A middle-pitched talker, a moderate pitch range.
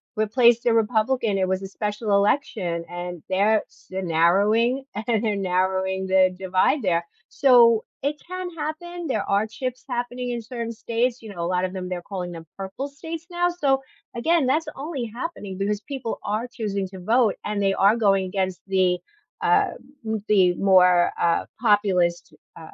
No: high, 210 Hz; average, 4.7 semitones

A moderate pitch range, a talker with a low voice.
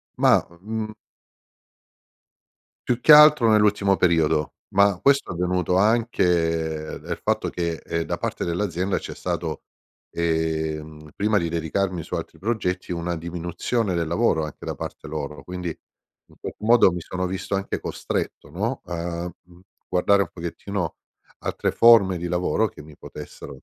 Yes: average, 3.5 semitones; very low, 90 Hz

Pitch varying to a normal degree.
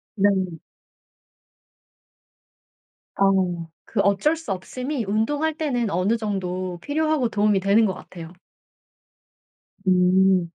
Yes: average, 4.5 semitones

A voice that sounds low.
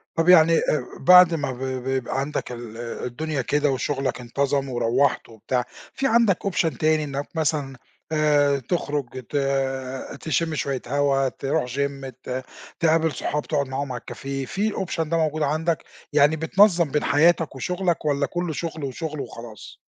No: medium, 145 Hz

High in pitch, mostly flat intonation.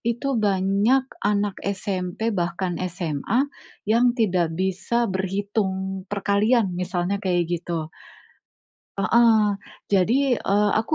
No: high, 195 Hz; average, 3.1 semitones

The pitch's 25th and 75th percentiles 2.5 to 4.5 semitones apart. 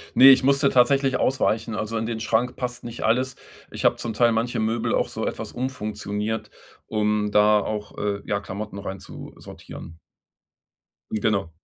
Yes: average, 2.8 semitones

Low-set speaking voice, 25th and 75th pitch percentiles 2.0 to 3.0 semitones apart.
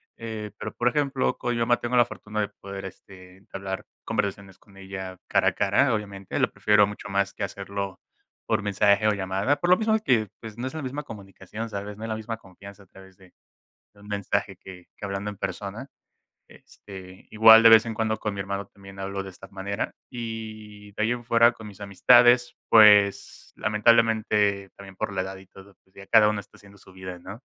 Yes: low, 100 Hz; narrow, 2.5 semitones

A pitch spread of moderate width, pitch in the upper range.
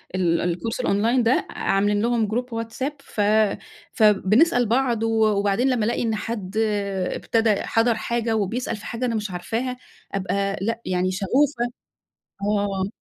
Yes: average, 3.0 semitones; high, 225 Hz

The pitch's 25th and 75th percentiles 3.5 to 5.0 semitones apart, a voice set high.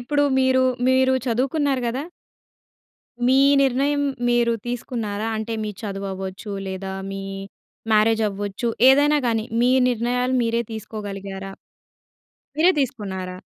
Yes: average, 4.3 semitones; high, 230 Hz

